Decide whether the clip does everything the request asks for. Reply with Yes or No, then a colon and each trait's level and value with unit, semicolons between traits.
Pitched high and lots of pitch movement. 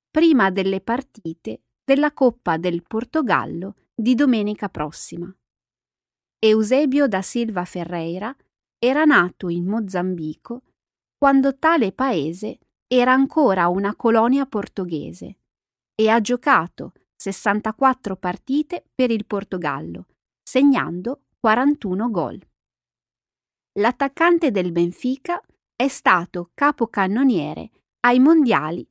Yes: high, 225 Hz; wide, 6.5 semitones